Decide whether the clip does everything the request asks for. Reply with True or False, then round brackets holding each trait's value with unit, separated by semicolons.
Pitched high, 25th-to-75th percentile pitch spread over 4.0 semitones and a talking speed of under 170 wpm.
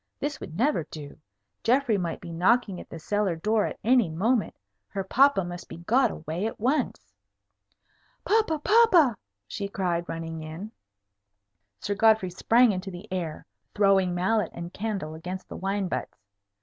True (195 Hz; 4.9 semitones; 155 wpm)